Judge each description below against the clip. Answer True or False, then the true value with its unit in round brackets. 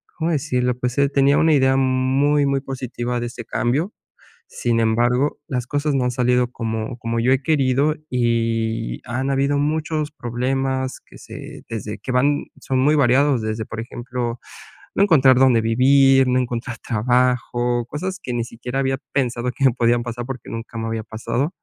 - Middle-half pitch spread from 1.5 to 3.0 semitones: True (2.5 semitones)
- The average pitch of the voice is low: True (125 Hz)